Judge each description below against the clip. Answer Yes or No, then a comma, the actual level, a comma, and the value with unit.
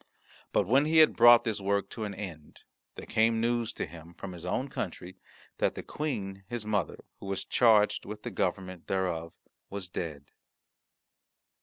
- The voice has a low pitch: Yes, low, 100 Hz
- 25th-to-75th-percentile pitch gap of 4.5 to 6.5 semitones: No, average, 4.1 semitones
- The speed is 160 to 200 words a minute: Yes, average, 170 wpm